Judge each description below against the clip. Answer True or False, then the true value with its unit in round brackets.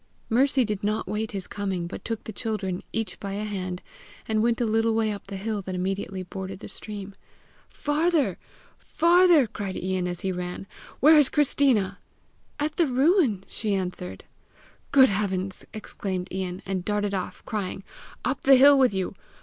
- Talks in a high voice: True (205 Hz)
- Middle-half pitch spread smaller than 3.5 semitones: False (4.7 semitones)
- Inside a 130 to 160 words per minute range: False (170 wpm)